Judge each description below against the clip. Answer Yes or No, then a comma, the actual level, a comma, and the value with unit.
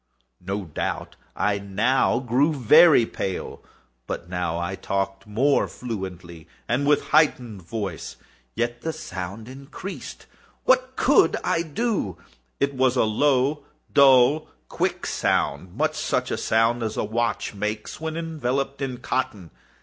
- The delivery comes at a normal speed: No, slow, 125 wpm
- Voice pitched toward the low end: Yes, low, 120 Hz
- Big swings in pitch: Yes, wide, 6.2 semitones